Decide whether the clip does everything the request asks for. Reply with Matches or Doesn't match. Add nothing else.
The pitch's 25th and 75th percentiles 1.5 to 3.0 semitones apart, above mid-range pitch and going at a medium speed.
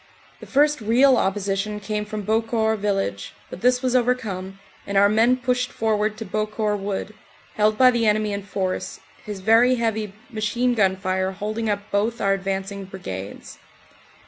Matches